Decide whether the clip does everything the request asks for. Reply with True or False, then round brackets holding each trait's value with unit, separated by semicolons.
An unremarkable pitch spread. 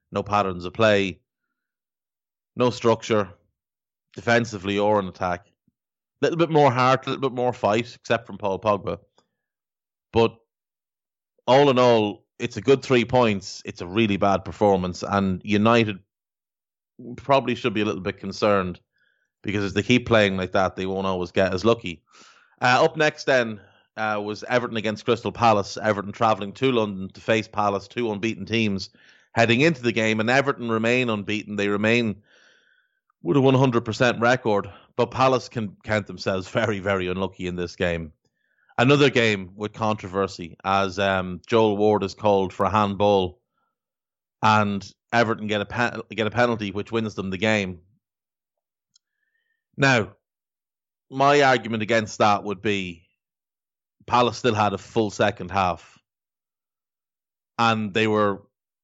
True (3.2 semitones)